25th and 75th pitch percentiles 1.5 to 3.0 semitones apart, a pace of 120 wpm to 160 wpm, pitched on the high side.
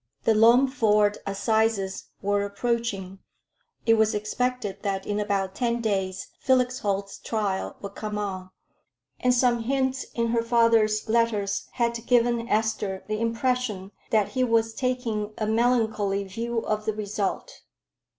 Yes: average, 2.7 semitones; slow, 135 wpm; high, 220 Hz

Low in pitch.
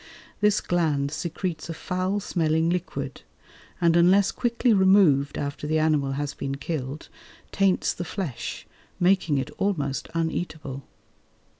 No: medium, 165 Hz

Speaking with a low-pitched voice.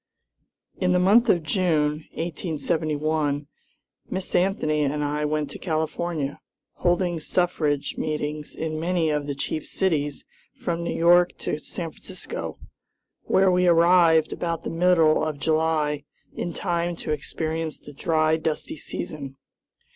No: medium, 160 Hz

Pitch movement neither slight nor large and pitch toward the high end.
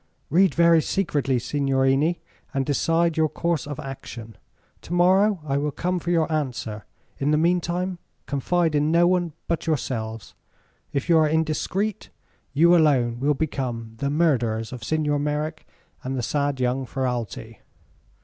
No: average, 4.2 semitones; medium, 150 Hz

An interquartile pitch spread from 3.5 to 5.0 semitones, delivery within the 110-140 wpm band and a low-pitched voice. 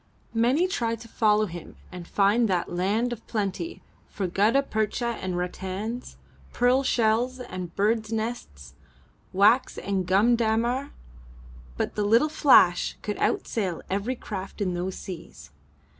No: average, 4.1 semitones; slow, 135 wpm; high, 215 Hz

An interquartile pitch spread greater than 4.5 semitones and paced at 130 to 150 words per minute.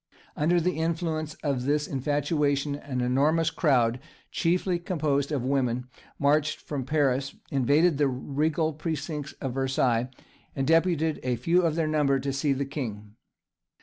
No: average, 3.0 semitones; average, 145 wpm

